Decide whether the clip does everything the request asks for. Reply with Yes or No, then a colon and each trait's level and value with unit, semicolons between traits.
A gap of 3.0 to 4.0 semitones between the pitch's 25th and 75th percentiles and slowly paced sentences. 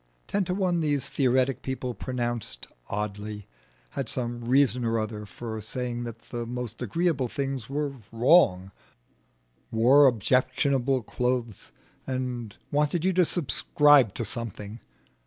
Yes: average, 3.3 semitones; slow, 125 wpm